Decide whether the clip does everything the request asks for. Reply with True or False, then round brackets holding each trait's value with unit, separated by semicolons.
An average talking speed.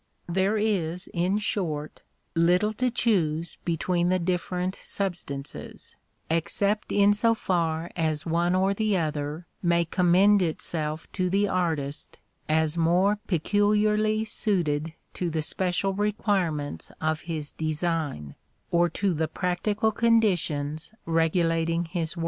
False (120 wpm)